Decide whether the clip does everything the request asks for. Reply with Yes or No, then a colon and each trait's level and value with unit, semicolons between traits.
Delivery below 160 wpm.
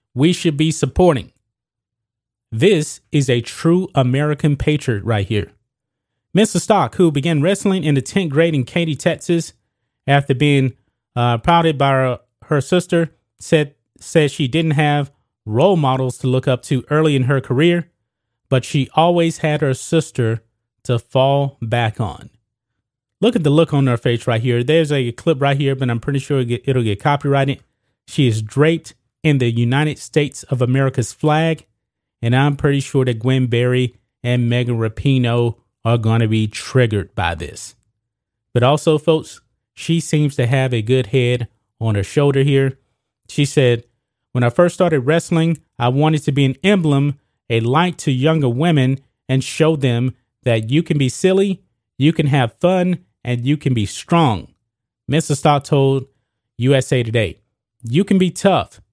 No: average, 165 wpm